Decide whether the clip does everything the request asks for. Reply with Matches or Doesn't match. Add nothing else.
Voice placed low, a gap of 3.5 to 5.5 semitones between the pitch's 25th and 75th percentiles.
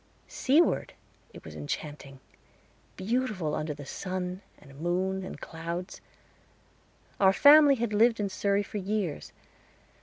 Doesn't match